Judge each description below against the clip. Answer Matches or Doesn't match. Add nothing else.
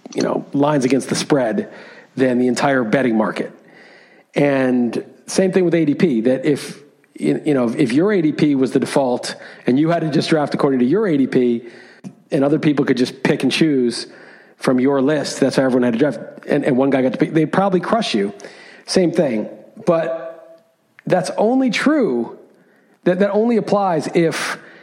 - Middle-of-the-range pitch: Matches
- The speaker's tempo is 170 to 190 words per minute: Matches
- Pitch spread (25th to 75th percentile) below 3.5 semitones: Doesn't match